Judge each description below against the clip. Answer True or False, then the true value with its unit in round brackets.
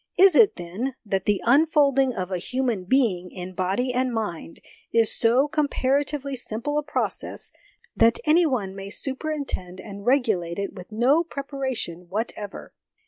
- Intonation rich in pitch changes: True (6.2 semitones)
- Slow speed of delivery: False (145 wpm)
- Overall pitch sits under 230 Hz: False (240 Hz)